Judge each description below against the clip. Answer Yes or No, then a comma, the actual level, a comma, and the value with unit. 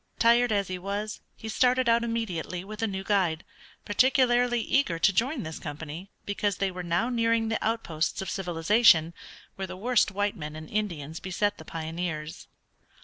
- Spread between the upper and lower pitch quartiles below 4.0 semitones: No, average, 5.1 semitones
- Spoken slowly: No, average, 170 wpm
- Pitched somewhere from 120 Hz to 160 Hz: No, high, 200 Hz